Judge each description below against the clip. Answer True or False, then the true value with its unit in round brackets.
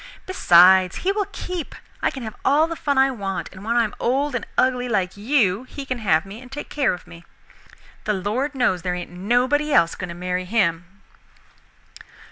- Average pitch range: False (6.7 semitones)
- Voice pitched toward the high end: True (230 Hz)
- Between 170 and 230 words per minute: True (200 wpm)